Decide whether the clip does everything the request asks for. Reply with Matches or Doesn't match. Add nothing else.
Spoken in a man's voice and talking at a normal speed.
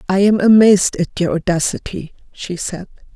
Doesn't match